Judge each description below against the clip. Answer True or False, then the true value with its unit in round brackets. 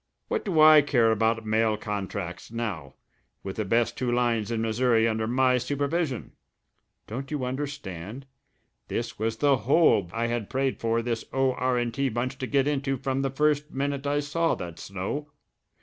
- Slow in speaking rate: False (175 wpm)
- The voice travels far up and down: False (3.7 semitones)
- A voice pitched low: True (125 Hz)